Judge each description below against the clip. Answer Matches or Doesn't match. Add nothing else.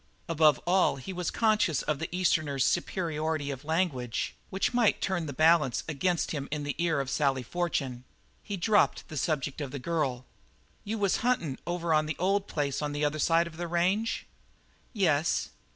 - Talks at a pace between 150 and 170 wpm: Doesn't match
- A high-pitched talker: Doesn't match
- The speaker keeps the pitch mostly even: Doesn't match